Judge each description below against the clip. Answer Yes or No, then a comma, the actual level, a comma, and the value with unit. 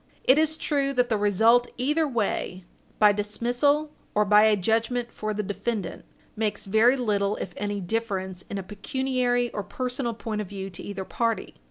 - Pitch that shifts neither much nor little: Yes, average, 3.2 semitones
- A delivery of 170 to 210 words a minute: Yes, average, 175 wpm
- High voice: Yes, high, 220 Hz